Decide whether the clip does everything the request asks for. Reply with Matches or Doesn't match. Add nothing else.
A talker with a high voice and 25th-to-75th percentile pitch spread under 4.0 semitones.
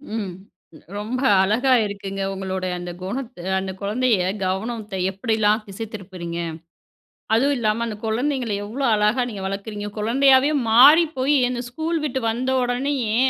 Doesn't match